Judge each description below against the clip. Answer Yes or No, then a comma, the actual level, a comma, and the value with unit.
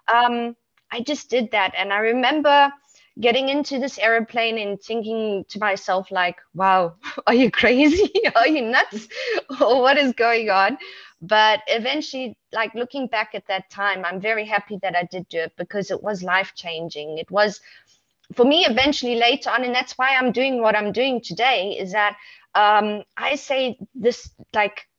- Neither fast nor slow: Yes, average, 175 wpm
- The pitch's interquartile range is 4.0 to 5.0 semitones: Yes, average, 4.3 semitones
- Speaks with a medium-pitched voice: No, high, 225 Hz